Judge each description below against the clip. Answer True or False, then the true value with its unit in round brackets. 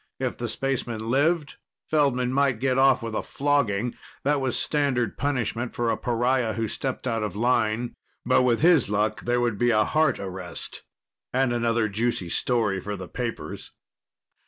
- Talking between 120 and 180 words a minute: True (165 wpm)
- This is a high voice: False (120 Hz)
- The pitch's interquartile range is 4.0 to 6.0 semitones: False (2.9 semitones)